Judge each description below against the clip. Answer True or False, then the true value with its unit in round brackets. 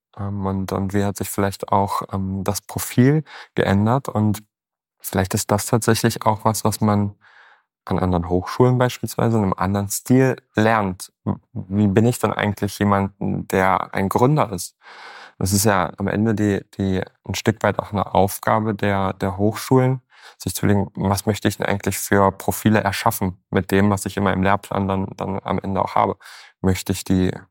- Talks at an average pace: True (180 wpm)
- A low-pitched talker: True (100 Hz)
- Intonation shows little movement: True (2.1 semitones)